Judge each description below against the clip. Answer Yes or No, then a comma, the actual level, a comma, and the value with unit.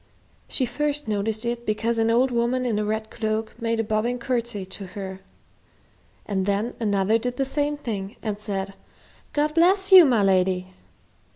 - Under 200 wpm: Yes, average, 170 wpm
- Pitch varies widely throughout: No, average, 3.4 semitones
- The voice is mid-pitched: No, high, 225 Hz